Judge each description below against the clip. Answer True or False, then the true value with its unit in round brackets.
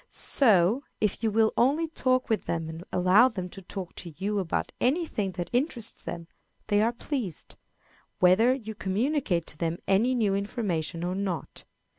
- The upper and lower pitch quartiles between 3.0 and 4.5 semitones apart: False (5.2 semitones)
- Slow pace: False (170 wpm)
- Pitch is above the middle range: True (205 Hz)